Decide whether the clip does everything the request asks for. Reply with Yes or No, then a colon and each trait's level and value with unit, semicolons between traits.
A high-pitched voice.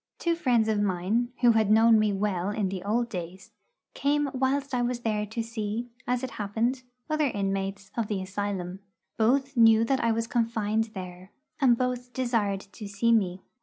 Yes: high, 220 Hz